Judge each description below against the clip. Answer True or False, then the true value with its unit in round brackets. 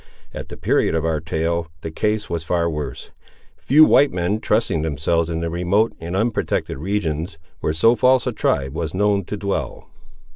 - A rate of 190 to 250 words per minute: False (180 wpm)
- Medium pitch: False (85 Hz)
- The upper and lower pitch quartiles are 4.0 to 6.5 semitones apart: True (4.5 semitones)